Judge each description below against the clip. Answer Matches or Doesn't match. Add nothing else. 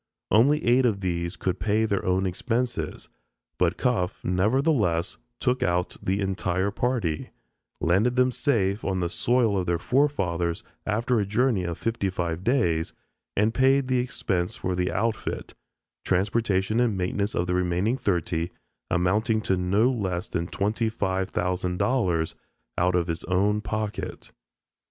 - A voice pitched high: Doesn't match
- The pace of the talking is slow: Doesn't match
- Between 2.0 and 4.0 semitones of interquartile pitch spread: Doesn't match